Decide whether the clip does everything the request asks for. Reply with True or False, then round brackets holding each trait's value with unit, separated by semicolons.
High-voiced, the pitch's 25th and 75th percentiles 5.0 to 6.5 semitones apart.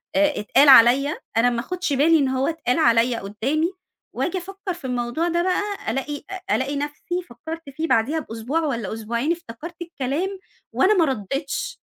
True (290 Hz; 5.6 semitones)